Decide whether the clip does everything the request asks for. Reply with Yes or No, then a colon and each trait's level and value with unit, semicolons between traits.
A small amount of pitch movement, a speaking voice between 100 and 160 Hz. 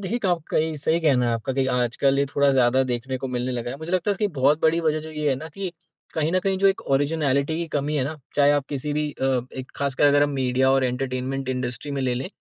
No: average, 3.3 semitones; medium, 140 Hz